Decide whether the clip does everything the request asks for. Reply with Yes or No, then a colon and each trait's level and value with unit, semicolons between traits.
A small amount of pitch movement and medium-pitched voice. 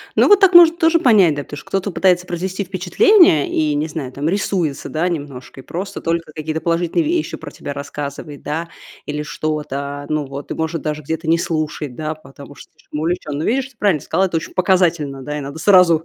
No: average, 3.9 semitones; medium, 160 Hz